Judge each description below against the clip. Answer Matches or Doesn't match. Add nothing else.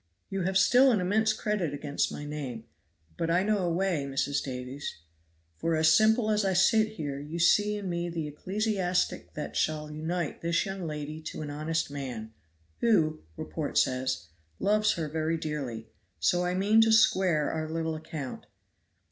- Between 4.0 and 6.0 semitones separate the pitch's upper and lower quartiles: Matches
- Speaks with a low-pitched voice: Doesn't match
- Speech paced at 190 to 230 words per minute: Doesn't match